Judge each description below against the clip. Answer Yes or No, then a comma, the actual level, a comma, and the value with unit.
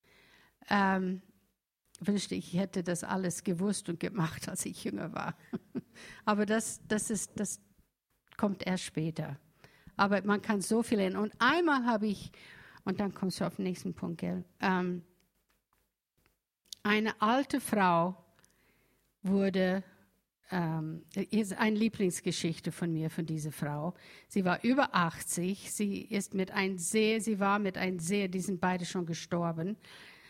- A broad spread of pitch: No, average, 2.9 semitones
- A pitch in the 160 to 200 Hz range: Yes, high, 190 Hz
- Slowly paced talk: No, average, 145 wpm